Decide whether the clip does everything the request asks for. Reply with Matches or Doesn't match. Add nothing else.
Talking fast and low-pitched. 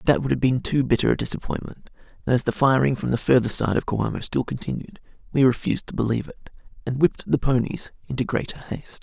Matches